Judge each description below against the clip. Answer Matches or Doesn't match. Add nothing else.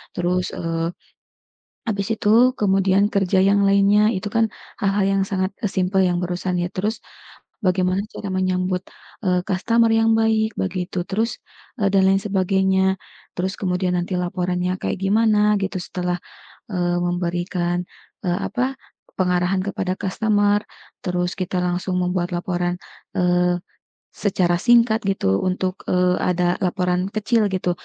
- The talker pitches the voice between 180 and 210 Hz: Matches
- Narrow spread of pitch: Matches